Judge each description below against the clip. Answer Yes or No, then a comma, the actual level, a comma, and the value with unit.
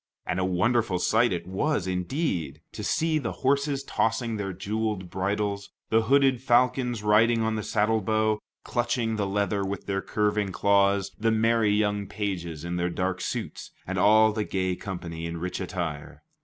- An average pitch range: Yes, average, 3.3 semitones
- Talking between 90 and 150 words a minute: No, average, 165 wpm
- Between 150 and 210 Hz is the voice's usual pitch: No, low, 105 Hz